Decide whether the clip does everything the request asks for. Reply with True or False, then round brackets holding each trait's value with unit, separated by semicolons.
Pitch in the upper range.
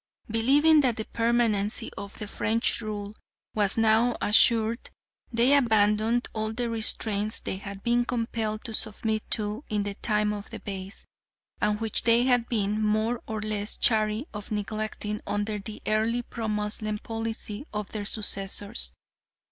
True (215 Hz)